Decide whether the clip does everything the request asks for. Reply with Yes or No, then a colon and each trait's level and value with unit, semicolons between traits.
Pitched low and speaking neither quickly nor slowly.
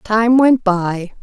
No: high, 215 Hz; average, 145 wpm